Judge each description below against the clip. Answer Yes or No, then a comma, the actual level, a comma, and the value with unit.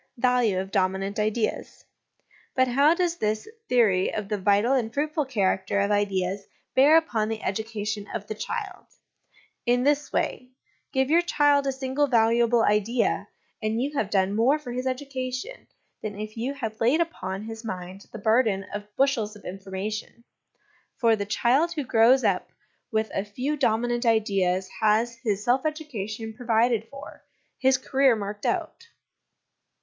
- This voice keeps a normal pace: Yes, average, 155 wpm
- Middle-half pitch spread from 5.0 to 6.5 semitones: No, average, 4.2 semitones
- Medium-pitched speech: No, high, 225 Hz